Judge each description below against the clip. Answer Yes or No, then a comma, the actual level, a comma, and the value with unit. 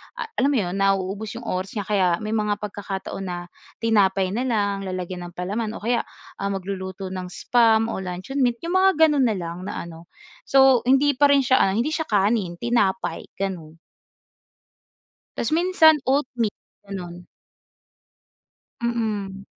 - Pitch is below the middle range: No, high, 205 Hz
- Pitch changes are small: No, average, 4.3 semitones